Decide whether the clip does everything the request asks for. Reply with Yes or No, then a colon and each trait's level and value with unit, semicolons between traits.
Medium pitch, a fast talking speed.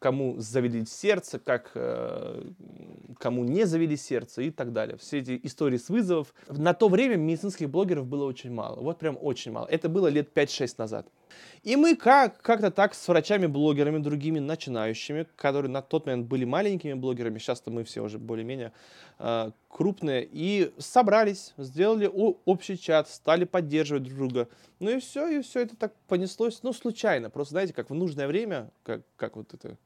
Yes: medium, 160 Hz; fast, 175 wpm